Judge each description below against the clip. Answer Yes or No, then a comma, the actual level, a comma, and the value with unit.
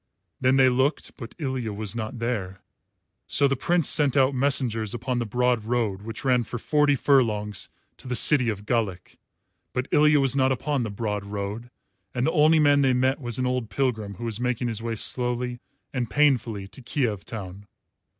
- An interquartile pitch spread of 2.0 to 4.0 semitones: Yes, average, 3.5 semitones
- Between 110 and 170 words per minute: No, average, 190 wpm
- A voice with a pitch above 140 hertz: No, low, 125 Hz